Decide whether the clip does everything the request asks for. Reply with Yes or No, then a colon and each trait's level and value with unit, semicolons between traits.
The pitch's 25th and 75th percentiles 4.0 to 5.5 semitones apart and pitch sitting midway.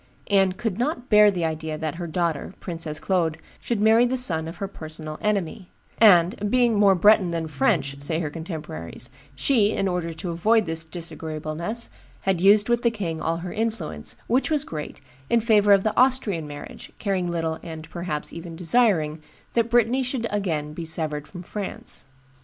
Yes: average, 5.1 semitones; medium, 180 Hz